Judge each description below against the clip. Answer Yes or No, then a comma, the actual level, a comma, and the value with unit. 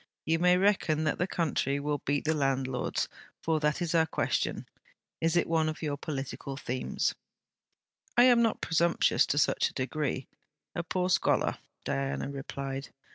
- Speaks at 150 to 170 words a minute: Yes, average, 160 wpm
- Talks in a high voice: No, medium, 155 Hz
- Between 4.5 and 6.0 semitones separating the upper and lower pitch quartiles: No, average, 3.7 semitones